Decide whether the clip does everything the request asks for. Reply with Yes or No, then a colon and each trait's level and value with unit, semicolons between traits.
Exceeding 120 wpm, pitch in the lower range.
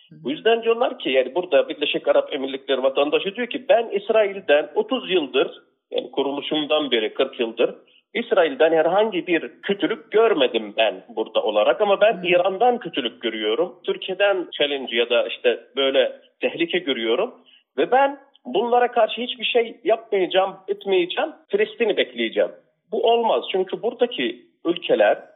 No: average, 135 wpm; high, 225 Hz